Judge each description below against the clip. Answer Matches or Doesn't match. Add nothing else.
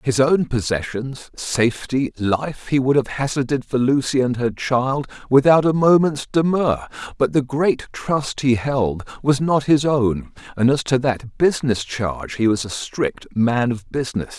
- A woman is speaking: Doesn't match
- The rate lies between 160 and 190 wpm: Matches